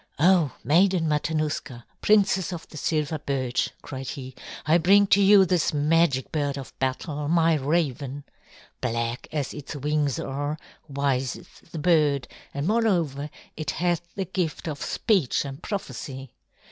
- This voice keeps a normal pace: Yes, average, 145 wpm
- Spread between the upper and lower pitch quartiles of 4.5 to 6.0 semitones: No, average, 3.8 semitones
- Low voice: No, medium, 150 Hz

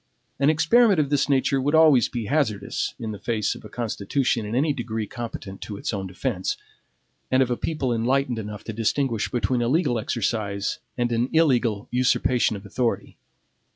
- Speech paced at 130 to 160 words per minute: No, average, 180 wpm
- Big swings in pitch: No, average, 4.2 semitones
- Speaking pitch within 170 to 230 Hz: No, low, 120 Hz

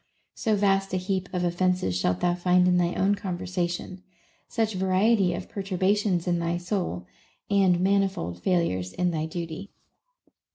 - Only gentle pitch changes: Yes, narrow, 2.0 semitones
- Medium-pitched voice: Yes, medium, 180 Hz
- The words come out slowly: No, average, 155 wpm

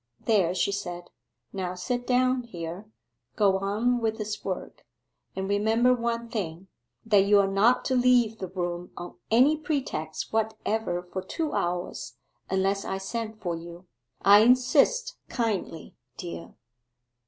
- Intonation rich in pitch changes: No, average, 4.6 semitones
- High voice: Yes, high, 205 Hz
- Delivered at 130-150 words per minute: Yes, average, 140 wpm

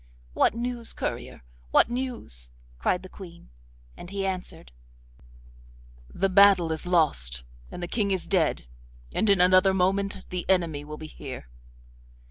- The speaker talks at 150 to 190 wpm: No, average, 140 wpm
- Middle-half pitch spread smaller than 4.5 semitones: Yes, average, 3.9 semitones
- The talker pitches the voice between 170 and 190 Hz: Yes, medium, 185 Hz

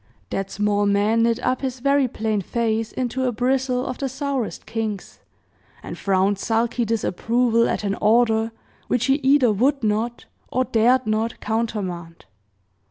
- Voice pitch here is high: Yes, high, 230 Hz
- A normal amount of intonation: Yes, average, 3.0 semitones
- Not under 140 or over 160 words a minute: Yes, average, 150 wpm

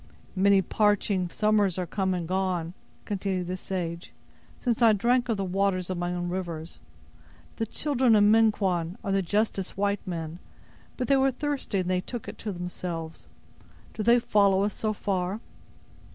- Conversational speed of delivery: Yes, average, 165 wpm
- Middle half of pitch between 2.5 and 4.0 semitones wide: Yes, average, 3.1 semitones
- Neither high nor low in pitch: No, high, 195 Hz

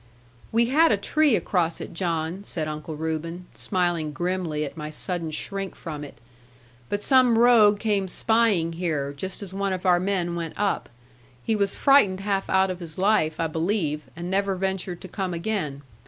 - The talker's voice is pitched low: No, medium, 185 Hz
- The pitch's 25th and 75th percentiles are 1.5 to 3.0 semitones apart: No, average, 3.6 semitones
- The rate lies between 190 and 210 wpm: No, average, 180 wpm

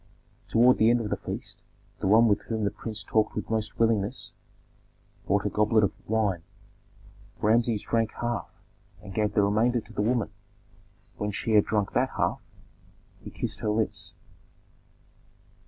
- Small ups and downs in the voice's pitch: Yes, narrow, 1.6 semitones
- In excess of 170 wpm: No, average, 155 wpm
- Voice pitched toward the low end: Yes, low, 110 Hz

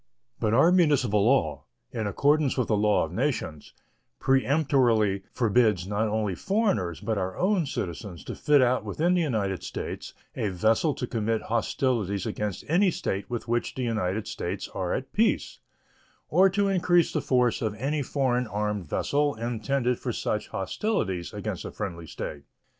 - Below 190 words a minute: Yes, average, 160 wpm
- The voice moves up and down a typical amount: No, wide, 5.8 semitones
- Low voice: Yes, low, 115 Hz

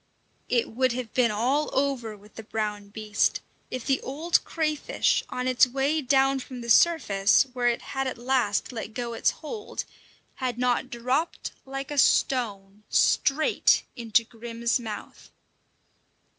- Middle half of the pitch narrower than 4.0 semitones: Yes, average, 3.2 semitones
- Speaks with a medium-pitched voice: No, very high, 250 Hz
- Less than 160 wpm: Yes, average, 145 wpm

